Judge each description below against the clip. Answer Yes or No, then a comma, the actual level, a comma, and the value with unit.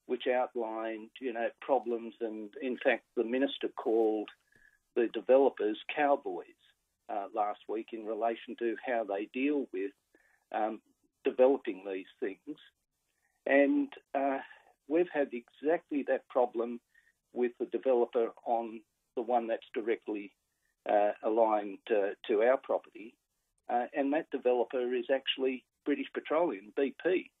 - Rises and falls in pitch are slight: No, average, 4.2 semitones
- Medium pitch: No, low, 125 Hz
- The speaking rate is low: Yes, slow, 125 wpm